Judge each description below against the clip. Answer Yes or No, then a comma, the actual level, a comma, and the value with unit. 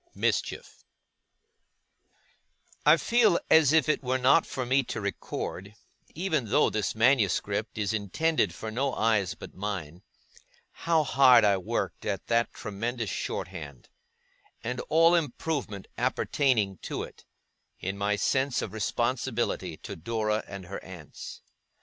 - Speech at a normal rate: No, slow, 130 wpm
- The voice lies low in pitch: Yes, low, 115 Hz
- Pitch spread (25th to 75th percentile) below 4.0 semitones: No, average, 5.2 semitones